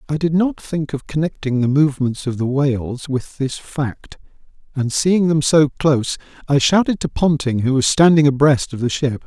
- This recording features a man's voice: Yes, male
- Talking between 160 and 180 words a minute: No, average, 195 wpm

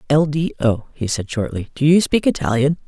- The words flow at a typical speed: No, fast, 210 wpm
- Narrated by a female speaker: Yes, female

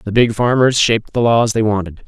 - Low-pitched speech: Yes, low, 110 Hz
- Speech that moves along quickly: Yes, fast, 230 wpm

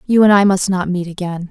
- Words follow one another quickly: Yes, fast, 280 wpm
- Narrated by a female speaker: Yes, female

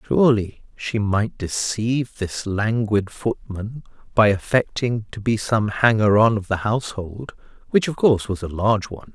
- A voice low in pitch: Yes, low, 110 Hz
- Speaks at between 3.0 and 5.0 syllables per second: Yes, 4.7 syllables/s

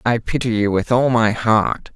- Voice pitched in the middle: No, low, 115 Hz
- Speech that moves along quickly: Yes, fast, 215 wpm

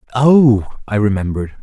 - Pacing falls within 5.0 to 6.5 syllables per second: Yes, 5.1 syllables/s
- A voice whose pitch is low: Yes, low, 115 Hz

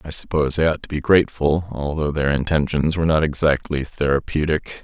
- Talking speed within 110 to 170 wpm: Yes, average, 150 wpm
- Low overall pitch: Yes, very low, 75 Hz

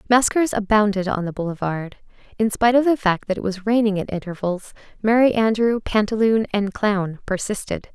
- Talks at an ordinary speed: Yes, average, 165 wpm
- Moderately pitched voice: No, high, 210 Hz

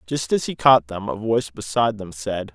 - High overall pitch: No, low, 105 Hz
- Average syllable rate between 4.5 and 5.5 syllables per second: Yes, 5.4 syllables/s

